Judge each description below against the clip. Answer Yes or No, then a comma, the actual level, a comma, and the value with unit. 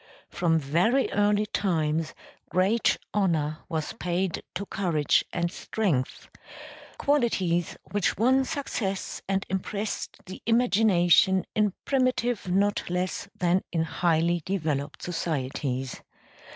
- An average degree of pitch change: Yes, average, 4.0 semitones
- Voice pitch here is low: No, medium, 185 Hz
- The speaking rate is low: Yes, slow, 105 wpm